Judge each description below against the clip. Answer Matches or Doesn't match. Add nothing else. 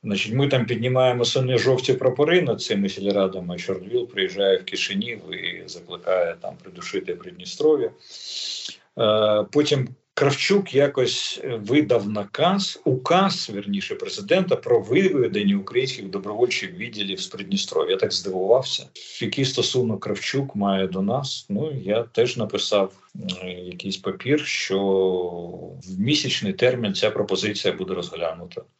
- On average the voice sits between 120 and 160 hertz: Matches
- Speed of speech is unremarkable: Matches